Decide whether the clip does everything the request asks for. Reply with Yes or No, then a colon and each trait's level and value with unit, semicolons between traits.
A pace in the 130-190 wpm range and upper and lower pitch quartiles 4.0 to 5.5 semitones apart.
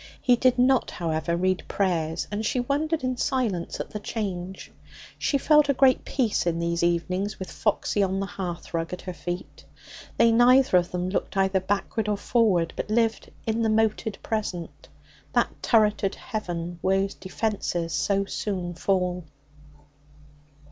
Yes: average, 155 wpm; average, 4.3 semitones